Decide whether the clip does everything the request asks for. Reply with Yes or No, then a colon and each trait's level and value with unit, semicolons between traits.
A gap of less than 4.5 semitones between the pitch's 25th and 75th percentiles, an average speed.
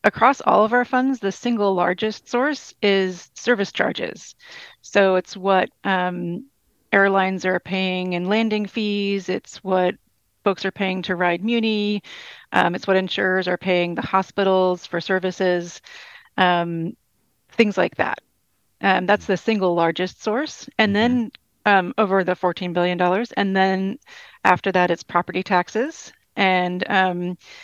Yes: average, 2.9 semitones; average, 145 wpm